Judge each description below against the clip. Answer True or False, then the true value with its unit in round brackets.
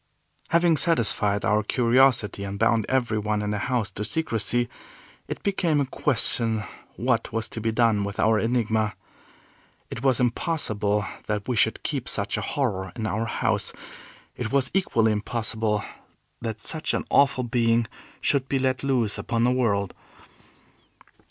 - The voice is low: True (115 Hz)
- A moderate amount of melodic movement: True (3.3 semitones)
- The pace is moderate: True (150 wpm)